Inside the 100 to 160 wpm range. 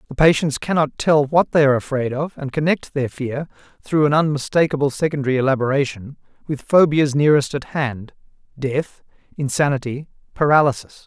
Yes: average, 140 wpm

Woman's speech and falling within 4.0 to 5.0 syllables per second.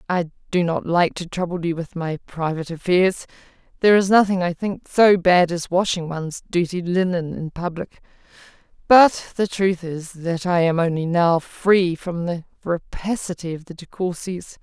Yes: female; 4.7 syllables/s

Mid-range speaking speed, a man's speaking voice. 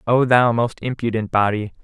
Yes: average, 165 wpm; male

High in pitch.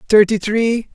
Yes: high, 215 Hz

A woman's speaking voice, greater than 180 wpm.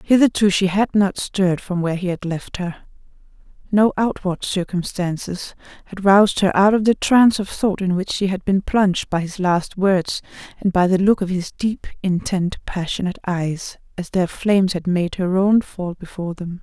Yes: female; average, 190 wpm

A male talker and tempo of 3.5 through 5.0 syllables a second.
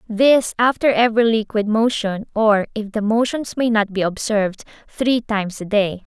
No: female; 4.8 syllables/s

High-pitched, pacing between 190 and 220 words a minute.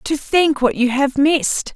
Yes: very high, 285 Hz; fast, 205 wpm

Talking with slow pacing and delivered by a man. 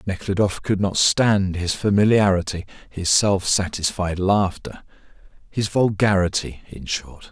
Yes: slow, 115 wpm; male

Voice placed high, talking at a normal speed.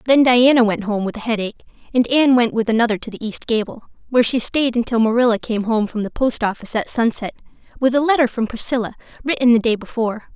No: high, 235 Hz; fast, 220 wpm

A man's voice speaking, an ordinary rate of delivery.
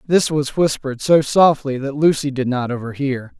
Yes: male; average, 175 wpm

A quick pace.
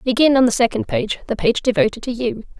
Yes: fast, 230 wpm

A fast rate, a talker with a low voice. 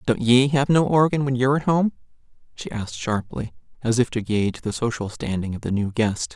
Yes: fast, 215 wpm; low, 120 Hz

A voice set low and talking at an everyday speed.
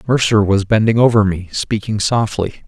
Yes: low, 105 Hz; average, 155 wpm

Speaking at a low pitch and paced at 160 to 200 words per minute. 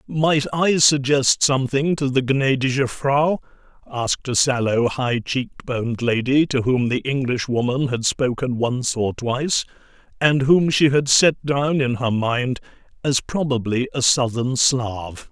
No: low, 130 Hz; average, 150 wpm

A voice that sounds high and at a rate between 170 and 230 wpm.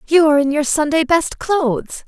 Yes: very high, 300 Hz; fast, 205 wpm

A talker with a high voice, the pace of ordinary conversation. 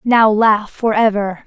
Yes: high, 215 Hz; average, 165 wpm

